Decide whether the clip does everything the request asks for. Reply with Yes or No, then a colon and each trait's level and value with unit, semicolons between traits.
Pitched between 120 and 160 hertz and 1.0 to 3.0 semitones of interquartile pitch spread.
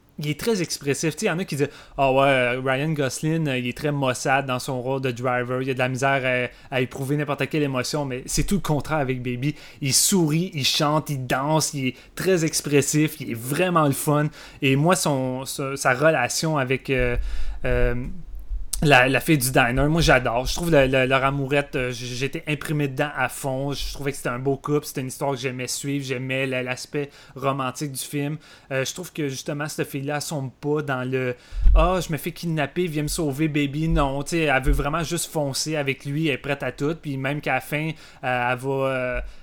Yes: medium, 140 Hz; narrow, 2.6 semitones